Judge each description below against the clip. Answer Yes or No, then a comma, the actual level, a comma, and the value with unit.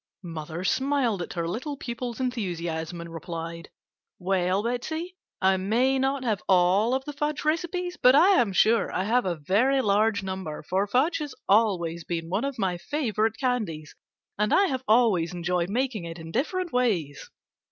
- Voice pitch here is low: No, high, 210 Hz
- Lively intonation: Yes, wide, 6.8 semitones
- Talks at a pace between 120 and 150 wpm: No, average, 170 wpm